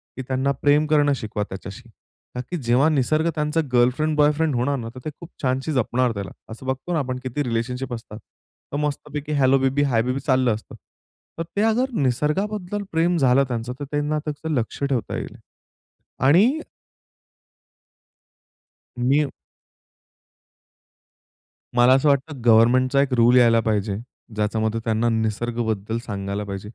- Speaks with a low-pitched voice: Yes, low, 130 Hz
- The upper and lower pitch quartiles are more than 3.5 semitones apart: Yes, average, 4.2 semitones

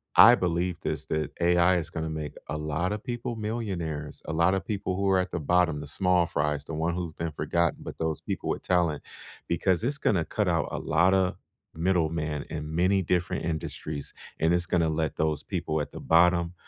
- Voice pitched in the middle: No, very low, 85 Hz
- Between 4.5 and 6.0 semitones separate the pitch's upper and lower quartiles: No, average, 2.7 semitones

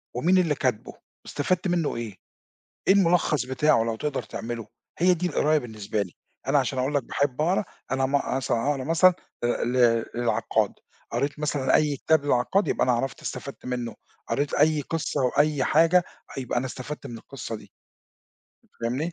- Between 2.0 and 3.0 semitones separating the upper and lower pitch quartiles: No, average, 4.1 semitones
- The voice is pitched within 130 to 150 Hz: Yes, medium, 140 Hz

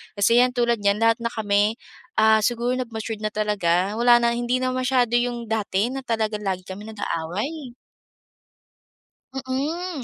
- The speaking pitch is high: Yes, high, 230 Hz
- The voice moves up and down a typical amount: Yes, average, 3.0 semitones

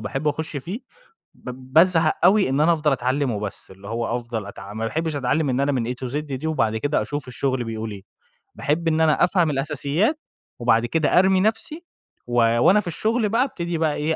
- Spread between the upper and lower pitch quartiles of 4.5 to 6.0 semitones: Yes, wide, 5.4 semitones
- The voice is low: No, medium, 145 Hz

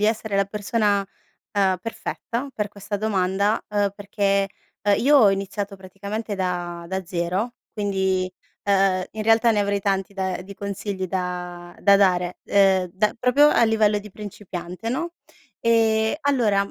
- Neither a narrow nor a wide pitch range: No, narrow, 2.3 semitones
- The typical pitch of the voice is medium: No, high, 200 Hz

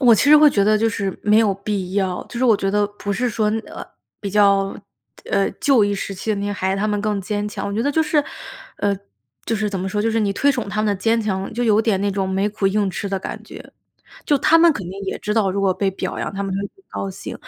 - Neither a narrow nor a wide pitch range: No, narrow, 2.2 semitones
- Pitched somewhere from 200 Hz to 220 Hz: Yes, high, 205 Hz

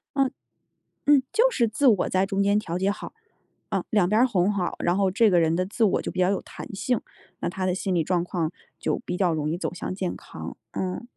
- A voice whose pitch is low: No, high, 190 Hz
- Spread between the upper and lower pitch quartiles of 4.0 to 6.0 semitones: No, average, 3.1 semitones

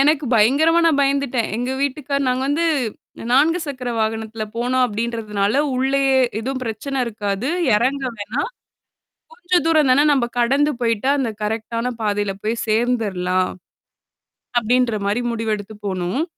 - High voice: Yes, high, 245 Hz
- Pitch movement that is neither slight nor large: Yes, average, 4.2 semitones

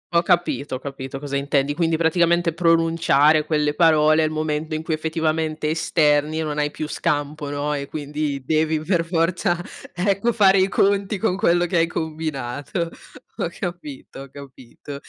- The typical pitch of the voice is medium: Yes, medium, 155 Hz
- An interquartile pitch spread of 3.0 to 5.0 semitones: No, narrow, 2.5 semitones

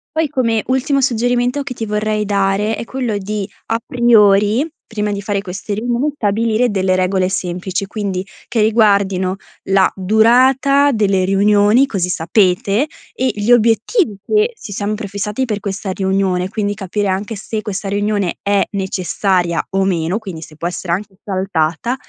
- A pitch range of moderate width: Yes, average, 3.0 semitones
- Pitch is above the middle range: Yes, high, 205 Hz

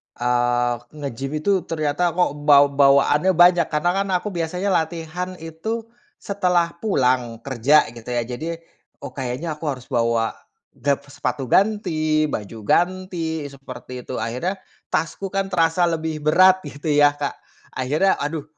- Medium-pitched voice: Yes, medium, 155 Hz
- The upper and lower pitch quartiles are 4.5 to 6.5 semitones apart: Yes, average, 4.8 semitones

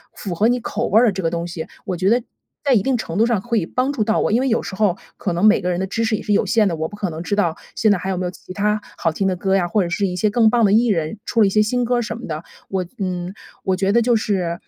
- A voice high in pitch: Yes, high, 200 Hz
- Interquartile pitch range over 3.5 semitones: Yes, average, 3.9 semitones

